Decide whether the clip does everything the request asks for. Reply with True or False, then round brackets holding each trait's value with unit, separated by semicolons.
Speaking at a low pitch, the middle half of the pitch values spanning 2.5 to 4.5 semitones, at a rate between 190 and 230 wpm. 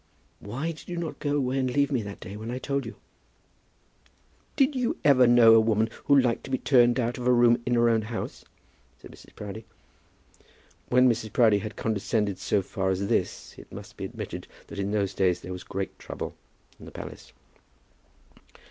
True (120 Hz; 3.7 semitones; 195 wpm)